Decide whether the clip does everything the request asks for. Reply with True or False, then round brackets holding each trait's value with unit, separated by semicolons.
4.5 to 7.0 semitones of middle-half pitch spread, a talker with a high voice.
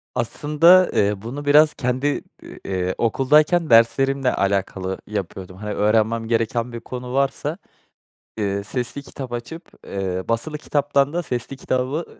False (5.2 semitones; 125 Hz)